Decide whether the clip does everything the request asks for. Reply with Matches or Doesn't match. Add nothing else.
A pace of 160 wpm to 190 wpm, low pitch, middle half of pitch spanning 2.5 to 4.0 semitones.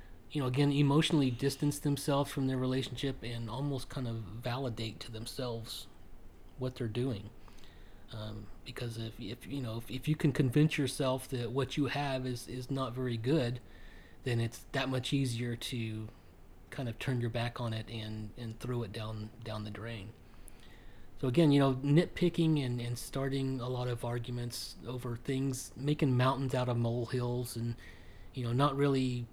Matches